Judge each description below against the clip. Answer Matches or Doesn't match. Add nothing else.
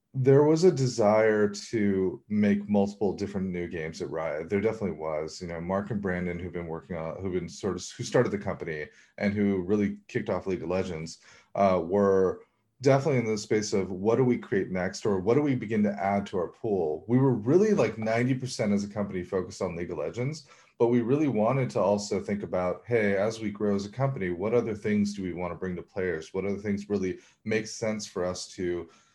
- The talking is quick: Matches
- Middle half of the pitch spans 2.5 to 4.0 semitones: Matches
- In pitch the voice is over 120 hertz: Doesn't match